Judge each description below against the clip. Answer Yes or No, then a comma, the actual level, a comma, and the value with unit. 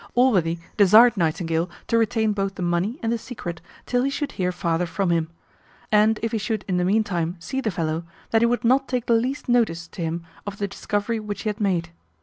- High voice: Yes, high, 205 Hz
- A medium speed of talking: No, fast, 220 wpm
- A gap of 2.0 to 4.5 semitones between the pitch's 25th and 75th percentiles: No, average, 4.9 semitones